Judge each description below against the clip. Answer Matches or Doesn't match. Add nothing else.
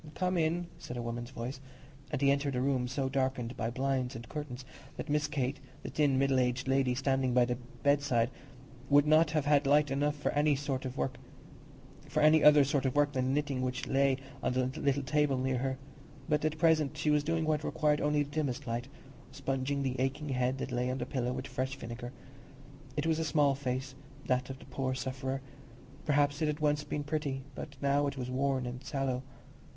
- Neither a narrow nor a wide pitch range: Doesn't match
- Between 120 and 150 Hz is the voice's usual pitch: Matches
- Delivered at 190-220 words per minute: Matches